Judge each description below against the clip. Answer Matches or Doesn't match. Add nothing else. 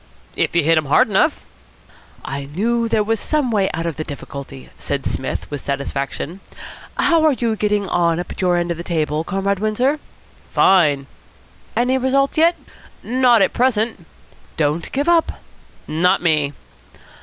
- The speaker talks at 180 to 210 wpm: Doesn't match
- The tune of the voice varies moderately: Doesn't match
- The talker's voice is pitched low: Doesn't match